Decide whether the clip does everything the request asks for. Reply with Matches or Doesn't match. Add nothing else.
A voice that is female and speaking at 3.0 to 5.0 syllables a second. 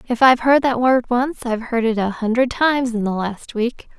Doesn't match